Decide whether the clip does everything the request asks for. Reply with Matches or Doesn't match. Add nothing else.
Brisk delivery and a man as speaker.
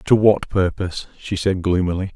Doesn't match